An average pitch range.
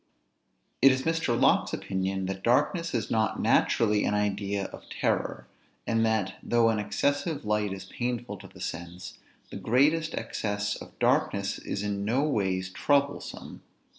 Yes: average, 4.5 semitones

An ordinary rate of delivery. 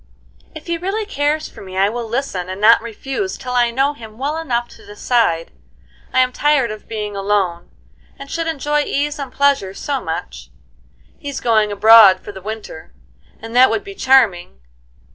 Yes: average, 175 wpm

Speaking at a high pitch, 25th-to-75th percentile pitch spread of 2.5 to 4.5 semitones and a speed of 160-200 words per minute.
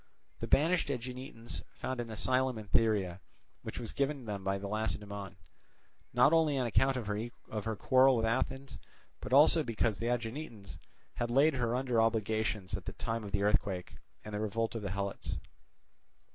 No: low, 115 Hz; average, 3.8 semitones; average, 170 wpm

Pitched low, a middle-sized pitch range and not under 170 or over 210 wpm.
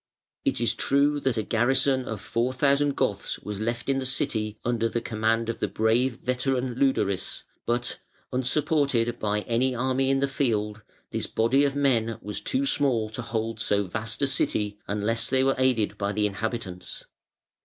Yes: low, 120 Hz; average, 3.4 semitones; average, 175 wpm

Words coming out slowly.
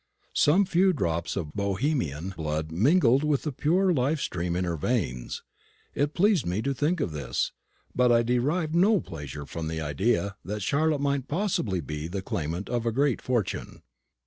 No: average, 175 wpm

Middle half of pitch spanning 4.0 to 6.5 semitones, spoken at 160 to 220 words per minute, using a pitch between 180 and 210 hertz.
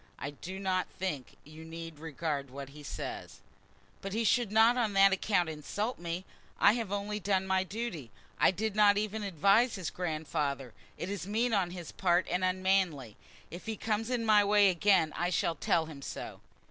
Yes: average, 4.3 semitones; average, 185 wpm; high, 190 Hz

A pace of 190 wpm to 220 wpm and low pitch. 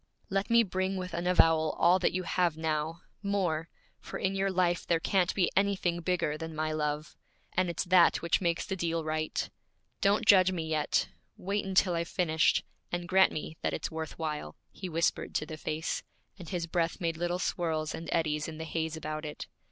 No: average, 200 wpm; medium, 170 Hz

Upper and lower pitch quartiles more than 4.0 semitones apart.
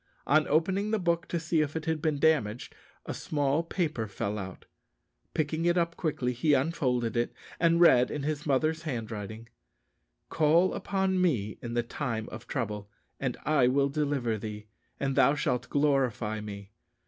Yes: wide, 5.5 semitones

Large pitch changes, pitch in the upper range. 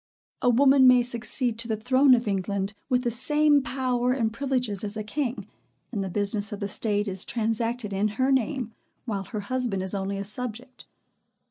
No: average, 3.7 semitones; high, 230 Hz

